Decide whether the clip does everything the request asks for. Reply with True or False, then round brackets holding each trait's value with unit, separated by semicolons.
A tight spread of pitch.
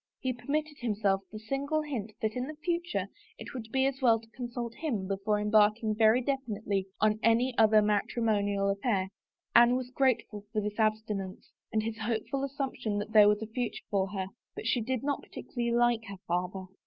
False (3.4 semitones)